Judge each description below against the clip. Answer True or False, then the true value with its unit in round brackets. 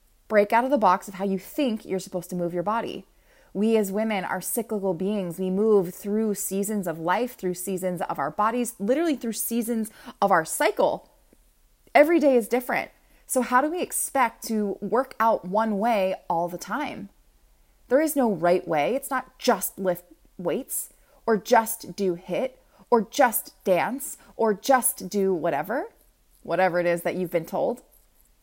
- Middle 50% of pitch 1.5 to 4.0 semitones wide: False (4.7 semitones)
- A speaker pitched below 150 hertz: False (210 Hz)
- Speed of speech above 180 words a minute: False (175 wpm)